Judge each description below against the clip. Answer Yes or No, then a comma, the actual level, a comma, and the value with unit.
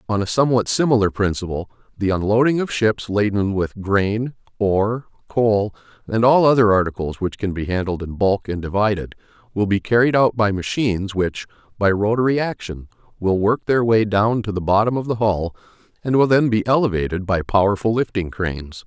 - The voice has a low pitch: Yes, low, 105 Hz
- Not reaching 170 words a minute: No, average, 180 wpm